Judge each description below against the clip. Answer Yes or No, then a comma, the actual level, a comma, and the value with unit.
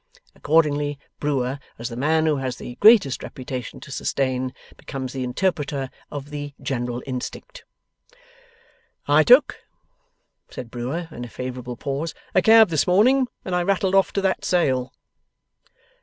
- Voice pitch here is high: No, medium, 145 Hz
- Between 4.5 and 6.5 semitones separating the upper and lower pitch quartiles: Yes, wide, 5.6 semitones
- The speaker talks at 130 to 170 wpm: Yes, average, 140 wpm